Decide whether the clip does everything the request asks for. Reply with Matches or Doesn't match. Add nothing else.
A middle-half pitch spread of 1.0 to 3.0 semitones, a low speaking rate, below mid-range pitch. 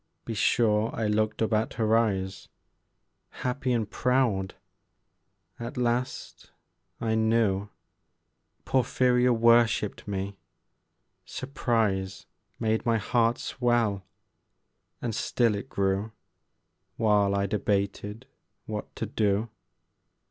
Matches